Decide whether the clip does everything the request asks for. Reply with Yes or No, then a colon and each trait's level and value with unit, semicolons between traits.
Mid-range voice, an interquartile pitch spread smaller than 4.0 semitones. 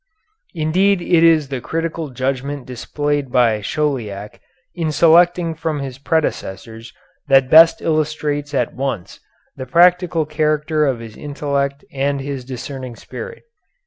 Yes: medium, 145 Hz; average, 3.5 semitones